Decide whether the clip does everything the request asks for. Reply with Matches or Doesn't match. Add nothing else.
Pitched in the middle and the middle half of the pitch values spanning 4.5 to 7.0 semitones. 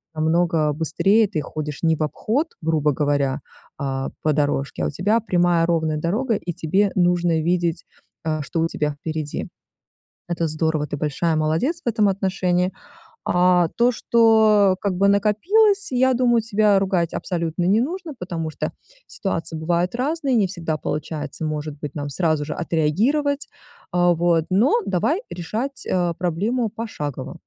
Matches